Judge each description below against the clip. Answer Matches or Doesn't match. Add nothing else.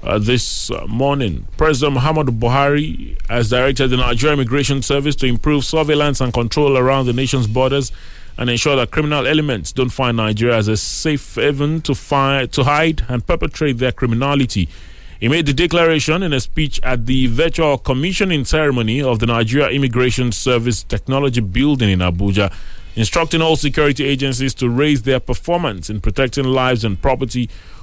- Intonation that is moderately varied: Matches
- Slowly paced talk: Doesn't match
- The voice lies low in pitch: Matches